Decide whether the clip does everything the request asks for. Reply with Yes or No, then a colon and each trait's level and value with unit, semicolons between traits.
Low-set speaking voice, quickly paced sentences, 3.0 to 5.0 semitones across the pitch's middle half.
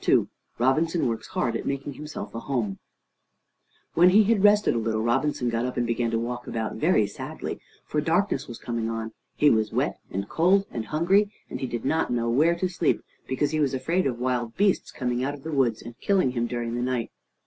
No: low, 130 Hz; fast, 215 wpm; wide, 5.5 semitones